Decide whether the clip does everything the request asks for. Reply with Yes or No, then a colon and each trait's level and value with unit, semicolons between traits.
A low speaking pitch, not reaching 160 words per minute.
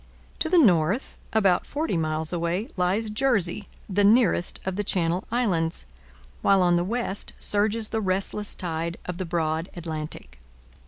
No: medium, 185 Hz; average, 150 wpm